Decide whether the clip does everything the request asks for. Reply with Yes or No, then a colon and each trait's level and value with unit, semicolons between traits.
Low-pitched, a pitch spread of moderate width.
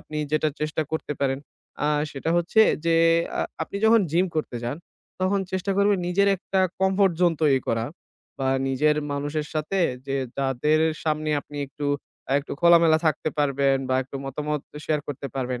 No: medium, 155 Hz; average, 3.8 semitones